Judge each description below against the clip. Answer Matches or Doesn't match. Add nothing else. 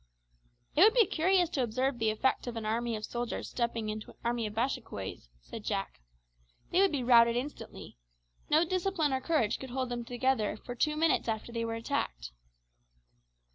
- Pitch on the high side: Matches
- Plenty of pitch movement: Doesn't match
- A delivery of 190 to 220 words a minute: Doesn't match